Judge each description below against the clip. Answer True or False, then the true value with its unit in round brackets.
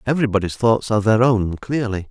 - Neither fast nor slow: True (170 wpm)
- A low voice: True (110 Hz)